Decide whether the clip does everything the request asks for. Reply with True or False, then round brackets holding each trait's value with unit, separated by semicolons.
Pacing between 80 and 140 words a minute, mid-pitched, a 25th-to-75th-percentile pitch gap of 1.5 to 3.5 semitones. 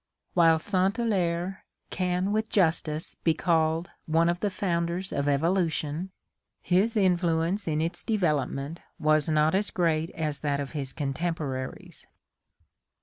True (135 wpm; 170 Hz; 3.1 semitones)